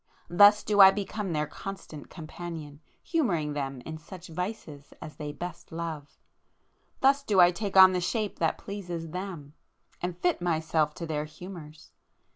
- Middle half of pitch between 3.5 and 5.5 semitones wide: Yes, average, 4.0 semitones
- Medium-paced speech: Yes, average, 150 wpm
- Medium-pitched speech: Yes, medium, 175 Hz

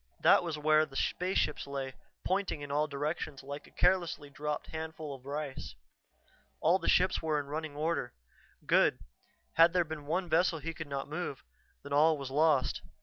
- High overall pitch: No, medium, 155 Hz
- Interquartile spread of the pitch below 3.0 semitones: Yes, narrow, 2.4 semitones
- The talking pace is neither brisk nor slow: Yes, average, 175 wpm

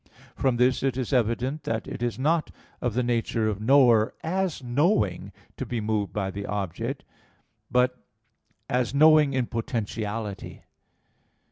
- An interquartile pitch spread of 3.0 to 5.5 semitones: Yes, average, 3.6 semitones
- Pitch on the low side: Yes, low, 120 Hz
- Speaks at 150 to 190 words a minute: No, average, 140 wpm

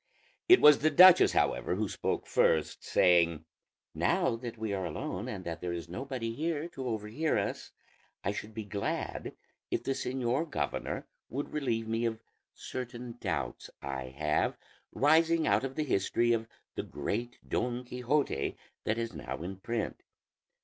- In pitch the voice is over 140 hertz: No, low, 115 Hz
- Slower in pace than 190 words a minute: Yes, average, 155 wpm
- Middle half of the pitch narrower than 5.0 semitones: No, wide, 5.4 semitones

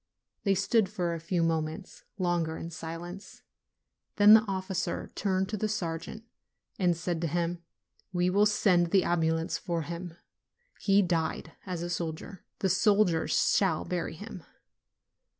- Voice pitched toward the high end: No, medium, 175 Hz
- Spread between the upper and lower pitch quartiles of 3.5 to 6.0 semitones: No, average, 2.9 semitones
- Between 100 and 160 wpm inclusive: Yes, average, 145 wpm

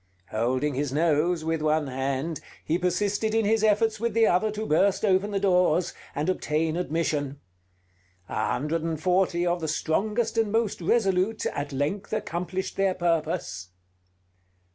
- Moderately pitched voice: Yes, medium, 175 Hz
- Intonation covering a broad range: No, average, 4.9 semitones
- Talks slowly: No, average, 150 wpm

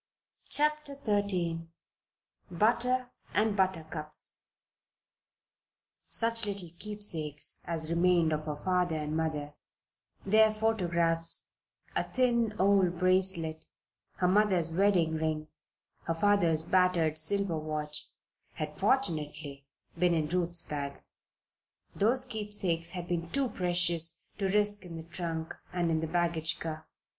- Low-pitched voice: No, medium, 175 Hz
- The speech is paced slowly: Yes, slow, 115 wpm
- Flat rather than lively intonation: No, average, 4.1 semitones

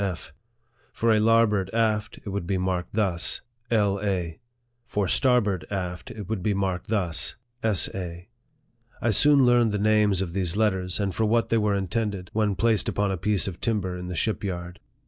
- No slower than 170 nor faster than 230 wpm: Yes, average, 200 wpm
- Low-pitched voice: Yes, low, 100 Hz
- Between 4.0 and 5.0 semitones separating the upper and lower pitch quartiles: No, average, 3.2 semitones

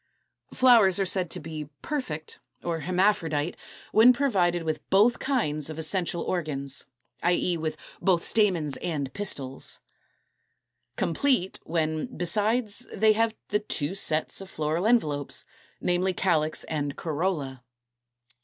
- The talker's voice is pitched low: No, medium, 175 Hz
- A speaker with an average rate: No, slow, 120 wpm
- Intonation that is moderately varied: Yes, average, 4.9 semitones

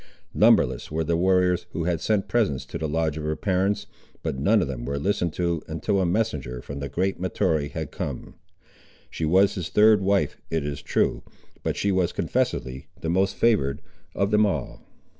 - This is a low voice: Yes, very low, 85 Hz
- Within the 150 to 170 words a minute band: No, average, 190 wpm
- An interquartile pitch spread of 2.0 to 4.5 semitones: No, average, 4.9 semitones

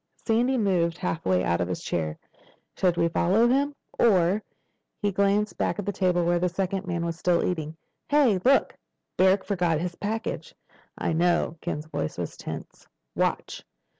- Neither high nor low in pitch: Yes, medium, 180 Hz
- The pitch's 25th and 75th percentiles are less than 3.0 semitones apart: No, average, 3.4 semitones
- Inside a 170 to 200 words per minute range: No, average, 160 wpm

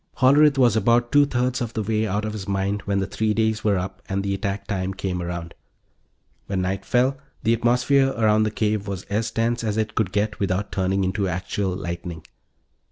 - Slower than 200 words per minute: No, fast, 205 wpm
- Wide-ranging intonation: No, average, 2.9 semitones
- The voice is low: Yes, low, 105 Hz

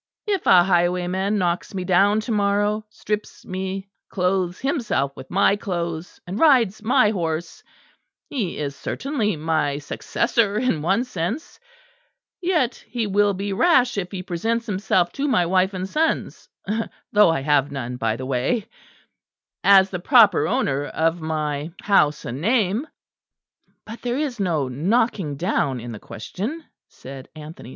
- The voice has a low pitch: No, high, 190 Hz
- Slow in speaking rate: No, average, 145 wpm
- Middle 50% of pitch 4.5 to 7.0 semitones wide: Yes, average, 5.3 semitones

